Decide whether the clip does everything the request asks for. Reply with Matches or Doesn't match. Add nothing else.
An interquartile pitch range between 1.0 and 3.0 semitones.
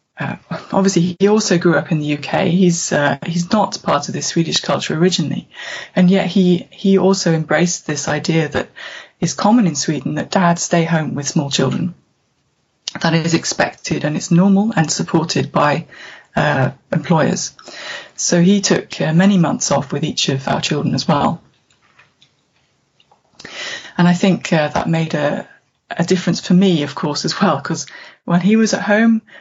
Doesn't match